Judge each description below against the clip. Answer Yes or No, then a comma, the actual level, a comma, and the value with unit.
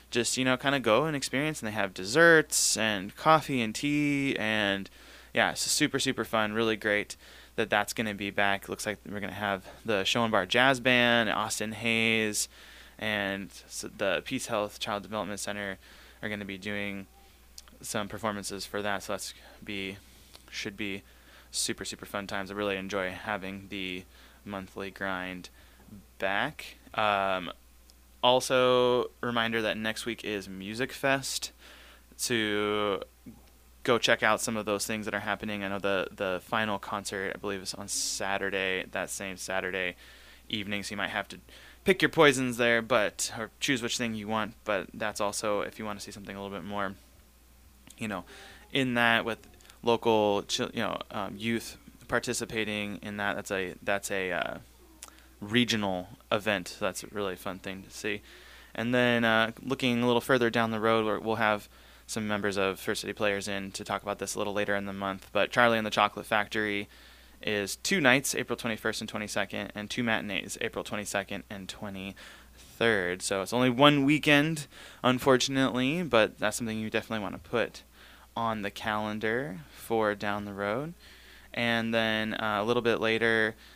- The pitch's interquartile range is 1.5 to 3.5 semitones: Yes, average, 2.9 semitones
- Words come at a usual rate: Yes, average, 175 wpm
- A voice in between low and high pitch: No, low, 105 Hz